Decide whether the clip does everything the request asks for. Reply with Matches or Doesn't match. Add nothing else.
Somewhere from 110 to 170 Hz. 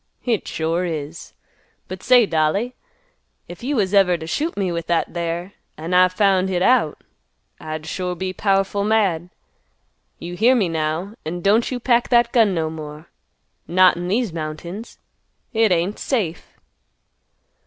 Doesn't match